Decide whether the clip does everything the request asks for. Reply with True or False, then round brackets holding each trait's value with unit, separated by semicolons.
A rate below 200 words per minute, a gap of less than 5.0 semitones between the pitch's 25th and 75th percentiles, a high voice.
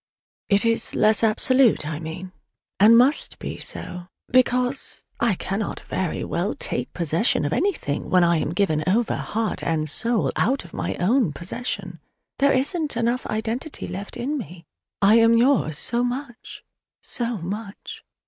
False (150 wpm; 5.6 semitones; 220 Hz)